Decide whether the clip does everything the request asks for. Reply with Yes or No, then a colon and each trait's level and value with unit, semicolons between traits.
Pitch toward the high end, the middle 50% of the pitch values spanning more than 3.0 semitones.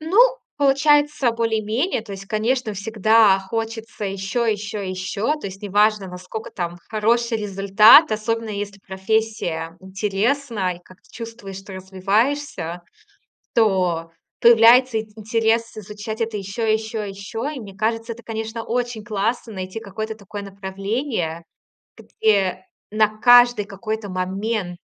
No: high, 215 Hz; average, 2.7 semitones